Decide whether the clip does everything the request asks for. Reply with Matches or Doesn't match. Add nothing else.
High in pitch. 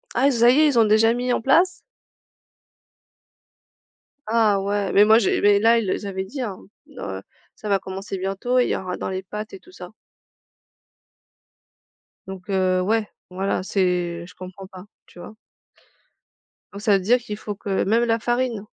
Matches